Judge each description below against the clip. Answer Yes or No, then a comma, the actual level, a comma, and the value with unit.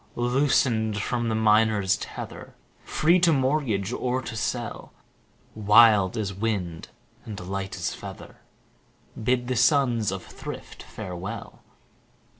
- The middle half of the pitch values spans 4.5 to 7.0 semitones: No, average, 3.8 semitones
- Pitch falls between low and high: No, low, 110 Hz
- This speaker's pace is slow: Yes, slow, 120 wpm